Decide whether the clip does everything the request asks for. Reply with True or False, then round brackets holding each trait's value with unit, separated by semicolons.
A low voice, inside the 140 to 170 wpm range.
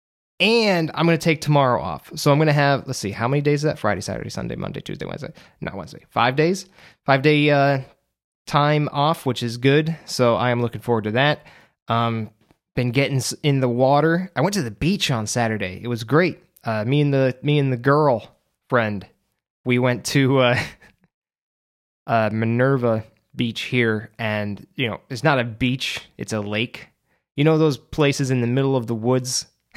False (130 Hz; 195 wpm)